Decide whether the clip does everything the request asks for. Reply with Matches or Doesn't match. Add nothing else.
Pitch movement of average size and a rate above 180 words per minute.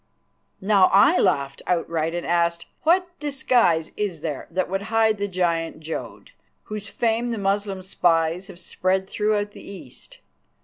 Doesn't match